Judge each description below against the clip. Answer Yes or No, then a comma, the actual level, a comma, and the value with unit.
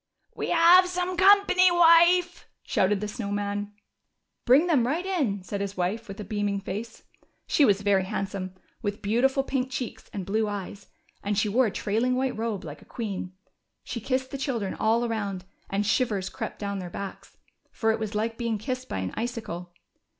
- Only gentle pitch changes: No, average, 4.6 semitones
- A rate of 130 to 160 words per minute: No, average, 185 wpm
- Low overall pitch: No, high, 220 Hz